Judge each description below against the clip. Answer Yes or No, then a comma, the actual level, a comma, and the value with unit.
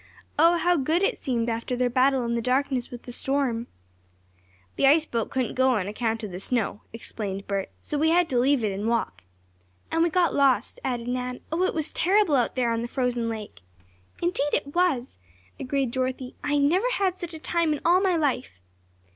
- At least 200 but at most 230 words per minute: Yes, fast, 205 wpm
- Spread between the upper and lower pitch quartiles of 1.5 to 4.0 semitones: No, average, 5.3 semitones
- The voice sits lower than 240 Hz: No, very high, 260 Hz